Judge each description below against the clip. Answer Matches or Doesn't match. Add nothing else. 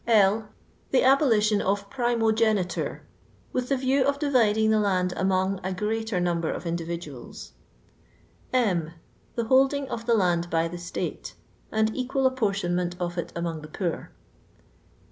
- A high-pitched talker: Matches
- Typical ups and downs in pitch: Matches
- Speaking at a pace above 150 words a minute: Doesn't match